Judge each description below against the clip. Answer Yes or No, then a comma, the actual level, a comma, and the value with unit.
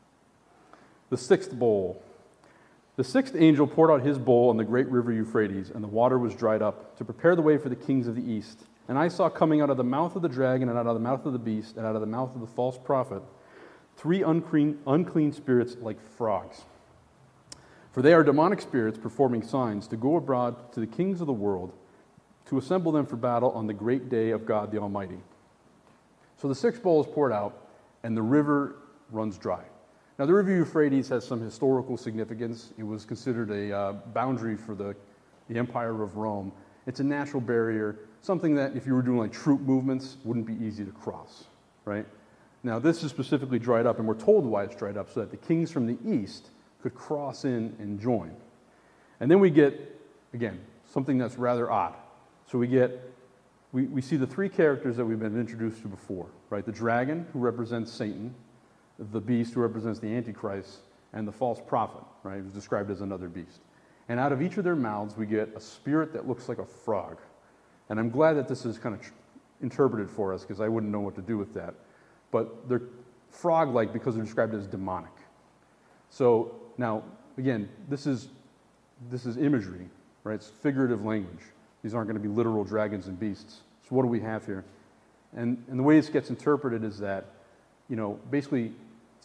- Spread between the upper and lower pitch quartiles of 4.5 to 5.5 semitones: No, average, 3.8 semitones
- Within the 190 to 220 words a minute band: Yes, average, 200 wpm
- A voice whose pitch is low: Yes, low, 120 Hz